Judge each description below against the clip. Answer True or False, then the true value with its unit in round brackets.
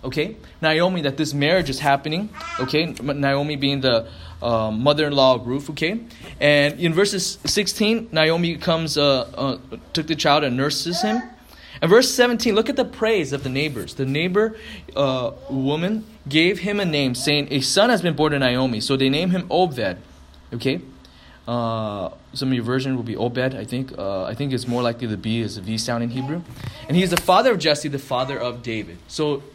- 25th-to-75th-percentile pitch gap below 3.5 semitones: False (5.1 semitones)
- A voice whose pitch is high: False (140 Hz)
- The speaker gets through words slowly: False (205 wpm)